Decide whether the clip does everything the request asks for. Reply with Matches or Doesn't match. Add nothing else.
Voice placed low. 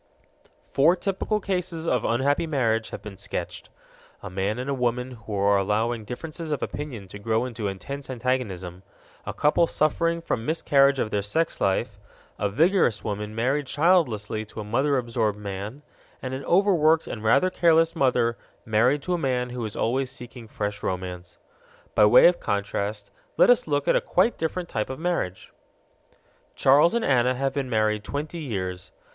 Matches